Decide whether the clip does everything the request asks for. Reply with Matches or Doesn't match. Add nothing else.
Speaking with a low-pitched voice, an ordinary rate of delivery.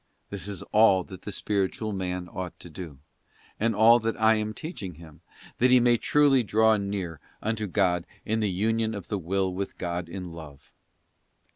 Matches